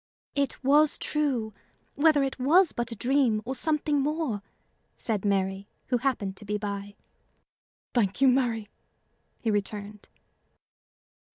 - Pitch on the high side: Yes, high, 240 Hz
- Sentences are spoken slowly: Yes, slow, 125 wpm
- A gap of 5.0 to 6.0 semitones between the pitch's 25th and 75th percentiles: Yes, wide, 5.4 semitones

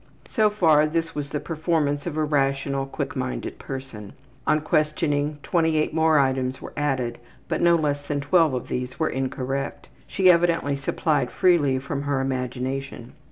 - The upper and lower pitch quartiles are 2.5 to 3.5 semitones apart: Yes, average, 2.9 semitones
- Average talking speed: Yes, average, 160 wpm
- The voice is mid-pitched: Yes, medium, 145 Hz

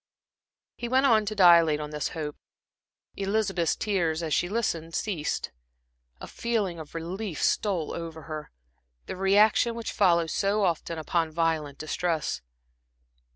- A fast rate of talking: No, slow, 135 wpm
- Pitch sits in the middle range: Yes, medium, 170 Hz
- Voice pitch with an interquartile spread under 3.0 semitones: No, average, 4.3 semitones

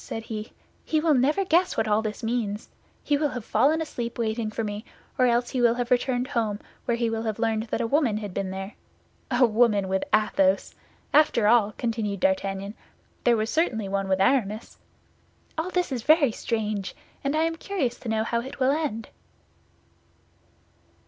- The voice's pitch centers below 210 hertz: No, high, 230 Hz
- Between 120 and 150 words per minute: No, average, 185 wpm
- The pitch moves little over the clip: No, average, 3.7 semitones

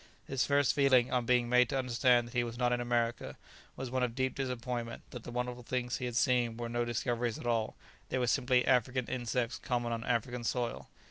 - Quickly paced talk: Yes, fast, 215 wpm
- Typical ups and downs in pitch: No, narrow, 1.2 semitones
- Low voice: Yes, low, 125 Hz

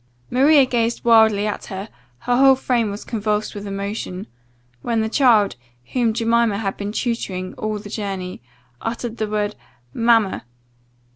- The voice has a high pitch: Yes, high, 220 Hz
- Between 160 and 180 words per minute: No, average, 145 wpm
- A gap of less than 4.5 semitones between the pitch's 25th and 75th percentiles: Yes, narrow, 2.6 semitones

